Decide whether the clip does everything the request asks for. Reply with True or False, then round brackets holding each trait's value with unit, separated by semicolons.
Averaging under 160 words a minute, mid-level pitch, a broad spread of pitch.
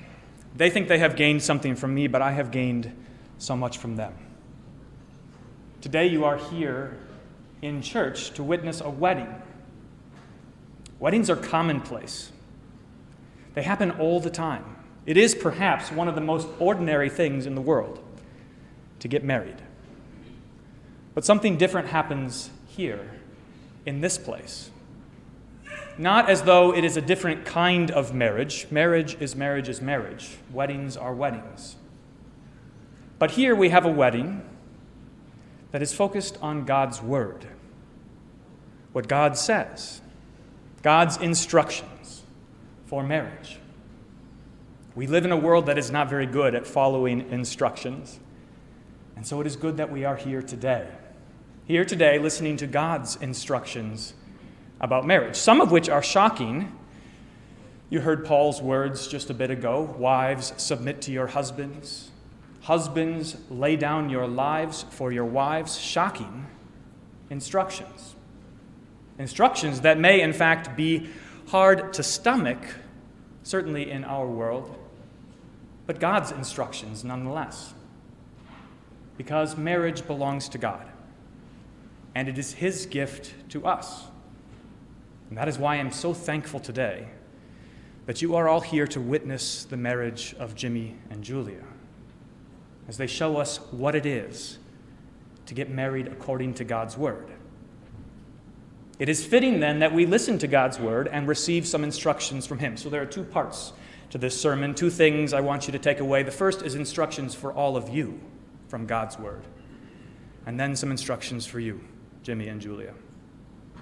False (140 wpm; 145 Hz; 3.8 semitones)